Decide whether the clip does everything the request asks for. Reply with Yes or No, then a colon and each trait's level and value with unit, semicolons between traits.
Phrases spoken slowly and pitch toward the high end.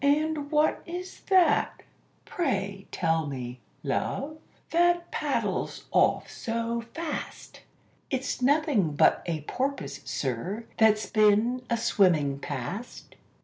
Yes: slow, 105 wpm; high, 230 Hz